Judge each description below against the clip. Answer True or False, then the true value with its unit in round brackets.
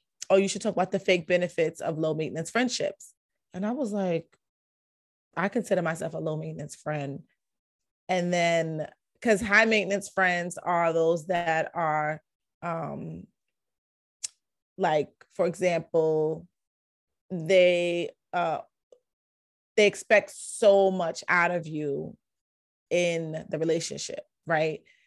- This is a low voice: False (175 Hz)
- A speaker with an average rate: False (120 wpm)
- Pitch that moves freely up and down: False (3.7 semitones)